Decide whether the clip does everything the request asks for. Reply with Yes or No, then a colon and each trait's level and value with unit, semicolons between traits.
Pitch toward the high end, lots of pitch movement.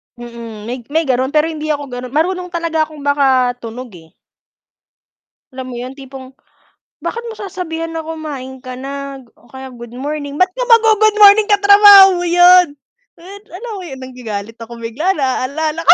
Yes: very high, 290 Hz; wide, 5.8 semitones